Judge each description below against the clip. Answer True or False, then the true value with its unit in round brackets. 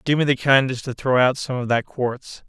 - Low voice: True (130 Hz)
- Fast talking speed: True (265 wpm)